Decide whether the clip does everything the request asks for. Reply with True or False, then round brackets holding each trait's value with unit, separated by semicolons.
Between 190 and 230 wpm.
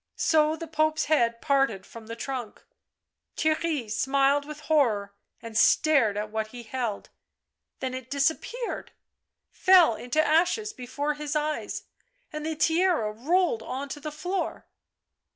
False (135 wpm)